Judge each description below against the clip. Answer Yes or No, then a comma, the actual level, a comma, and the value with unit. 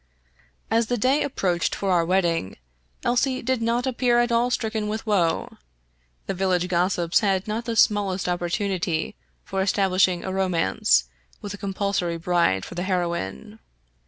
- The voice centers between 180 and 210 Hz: Yes, high, 190 Hz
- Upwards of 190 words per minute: No, average, 150 wpm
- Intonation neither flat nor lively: Yes, average, 4.1 semitones